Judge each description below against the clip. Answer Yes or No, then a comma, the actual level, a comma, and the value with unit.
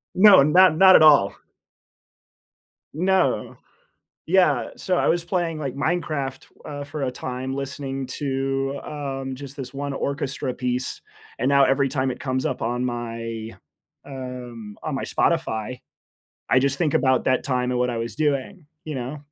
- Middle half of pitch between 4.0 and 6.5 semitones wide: No, average, 2.9 semitones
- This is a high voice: No, low, 135 Hz